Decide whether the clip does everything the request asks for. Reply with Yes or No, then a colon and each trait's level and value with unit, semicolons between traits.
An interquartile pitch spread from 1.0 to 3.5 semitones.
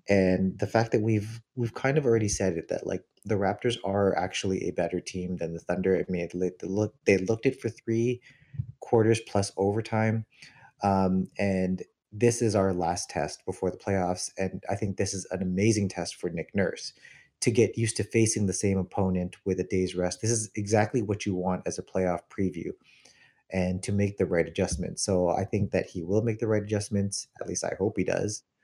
Yes: average, 3.2 semitones